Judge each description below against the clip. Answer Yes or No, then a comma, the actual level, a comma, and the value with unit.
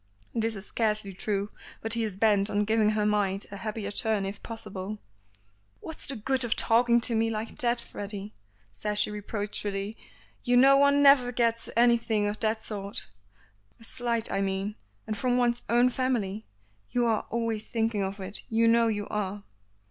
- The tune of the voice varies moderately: No, narrow, 2.3 semitones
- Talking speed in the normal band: Yes, average, 175 wpm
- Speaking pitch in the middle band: No, high, 220 Hz